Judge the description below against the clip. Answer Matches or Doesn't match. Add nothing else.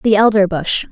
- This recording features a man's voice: Doesn't match